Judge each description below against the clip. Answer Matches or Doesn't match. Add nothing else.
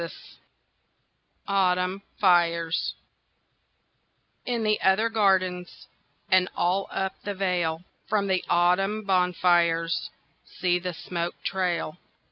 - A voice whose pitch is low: Doesn't match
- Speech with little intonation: Matches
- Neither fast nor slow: Doesn't match